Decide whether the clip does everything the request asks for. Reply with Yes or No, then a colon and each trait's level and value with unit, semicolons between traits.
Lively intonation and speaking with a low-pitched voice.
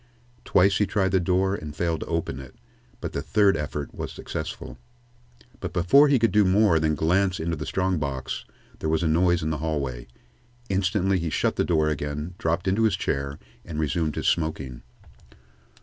No: average, 3.8 semitones; very low, 85 Hz